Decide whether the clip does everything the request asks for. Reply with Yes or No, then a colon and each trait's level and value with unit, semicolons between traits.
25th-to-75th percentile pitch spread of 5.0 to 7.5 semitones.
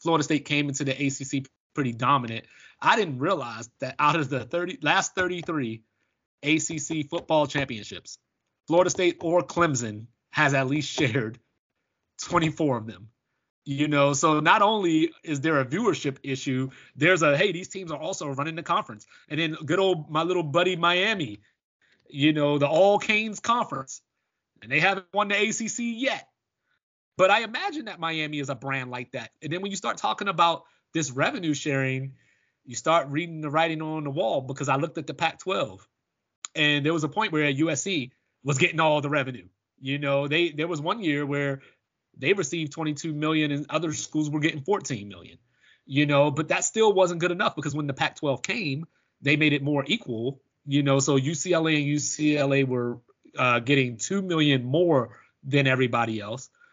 No: average, 3.7 semitones